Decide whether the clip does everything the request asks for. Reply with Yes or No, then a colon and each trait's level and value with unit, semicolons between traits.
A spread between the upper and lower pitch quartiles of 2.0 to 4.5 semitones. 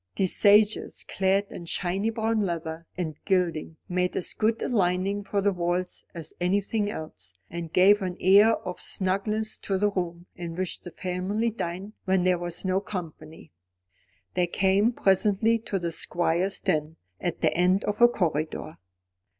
Yes: average, 2.8 semitones